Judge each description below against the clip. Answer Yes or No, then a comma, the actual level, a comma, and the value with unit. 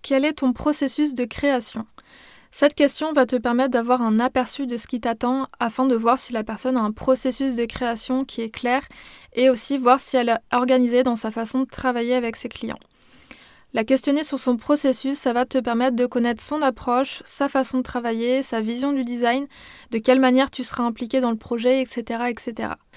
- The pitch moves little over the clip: Yes, narrow, 1.9 semitones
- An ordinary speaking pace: Yes, average, 205 wpm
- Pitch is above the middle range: Yes, very high, 255 Hz